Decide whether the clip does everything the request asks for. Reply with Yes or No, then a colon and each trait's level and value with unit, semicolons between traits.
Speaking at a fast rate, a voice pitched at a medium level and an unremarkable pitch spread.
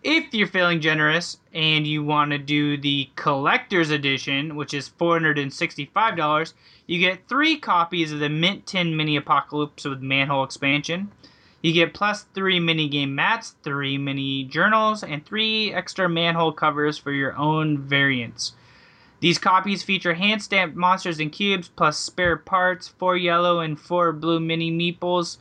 No: average, 155 wpm; medium, 165 Hz; average, 3.7 semitones